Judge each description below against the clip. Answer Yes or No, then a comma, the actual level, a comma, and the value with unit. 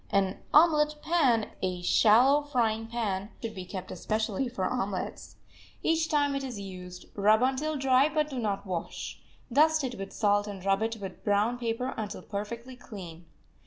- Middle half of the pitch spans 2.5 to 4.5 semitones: No, average, 5.1 semitones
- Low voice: No, high, 225 Hz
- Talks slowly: No, average, 165 wpm